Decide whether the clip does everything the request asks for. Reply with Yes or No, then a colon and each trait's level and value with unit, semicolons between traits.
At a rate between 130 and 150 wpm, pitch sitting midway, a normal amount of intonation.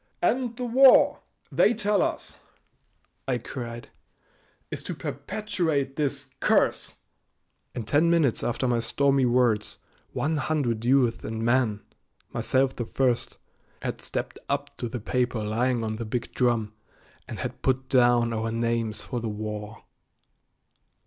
No: slow, 135 wpm; low, 125 Hz; average, 3.5 semitones